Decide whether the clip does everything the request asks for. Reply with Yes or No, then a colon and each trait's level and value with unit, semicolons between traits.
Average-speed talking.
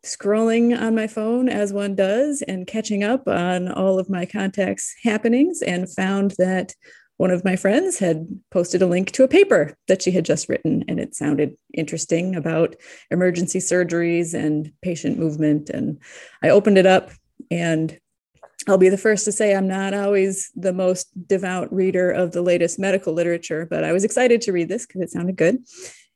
Yes: average, 185 wpm